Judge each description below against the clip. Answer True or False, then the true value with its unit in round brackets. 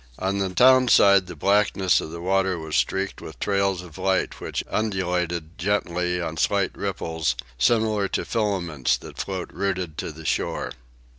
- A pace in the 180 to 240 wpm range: False (160 wpm)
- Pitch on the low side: True (95 Hz)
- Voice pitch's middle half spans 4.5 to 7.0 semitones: False (2.8 semitones)